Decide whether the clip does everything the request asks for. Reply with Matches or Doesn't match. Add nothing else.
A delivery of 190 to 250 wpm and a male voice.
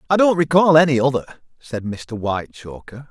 Doesn't match